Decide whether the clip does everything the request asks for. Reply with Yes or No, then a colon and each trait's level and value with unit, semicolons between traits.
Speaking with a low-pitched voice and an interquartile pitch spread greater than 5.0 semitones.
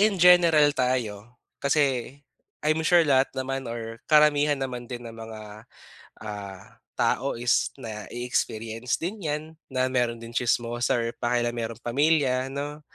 No: low, 125 Hz; average, 3.9 semitones